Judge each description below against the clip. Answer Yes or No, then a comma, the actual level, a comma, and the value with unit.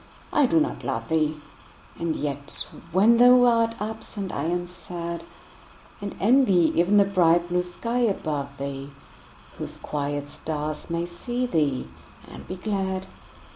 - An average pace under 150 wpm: Yes, average, 140 wpm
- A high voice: No, medium, 175 Hz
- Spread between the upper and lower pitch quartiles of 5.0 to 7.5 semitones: Yes, wide, 5.6 semitones